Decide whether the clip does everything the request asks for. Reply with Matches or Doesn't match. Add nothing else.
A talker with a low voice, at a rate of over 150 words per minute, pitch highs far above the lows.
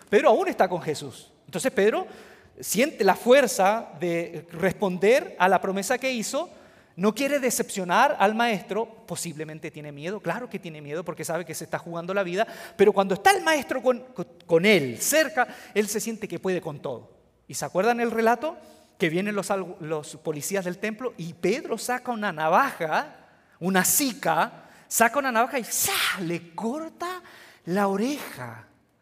Doesn't match